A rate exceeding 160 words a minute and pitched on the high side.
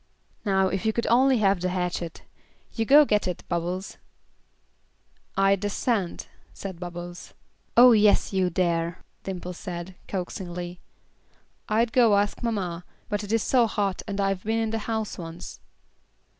No: average, 145 wpm; high, 195 Hz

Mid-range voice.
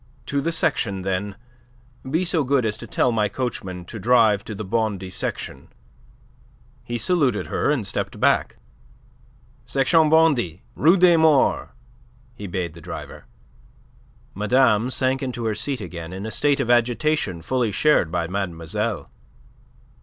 No: low, 115 Hz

